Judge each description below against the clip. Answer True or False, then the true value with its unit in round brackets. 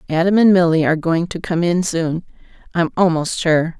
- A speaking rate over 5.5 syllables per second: False (5.3 syllables/s)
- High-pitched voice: False (170 Hz)